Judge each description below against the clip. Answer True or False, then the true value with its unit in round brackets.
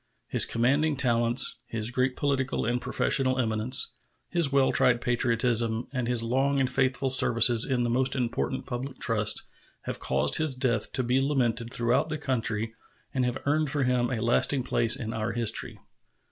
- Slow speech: False (170 wpm)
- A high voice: False (125 Hz)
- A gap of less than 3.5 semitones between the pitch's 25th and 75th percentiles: True (2.4 semitones)